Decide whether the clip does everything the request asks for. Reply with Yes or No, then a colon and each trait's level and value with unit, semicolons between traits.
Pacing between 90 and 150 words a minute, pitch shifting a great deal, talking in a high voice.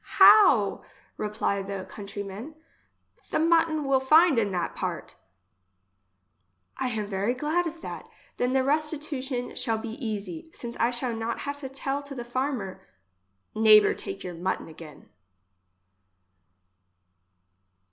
Yes: slow, 135 wpm; wide, 6.0 semitones; high, 240 Hz